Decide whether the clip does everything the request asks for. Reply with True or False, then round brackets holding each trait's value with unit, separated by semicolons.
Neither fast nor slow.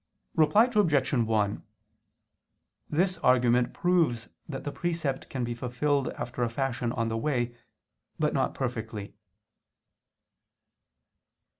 False (110 wpm)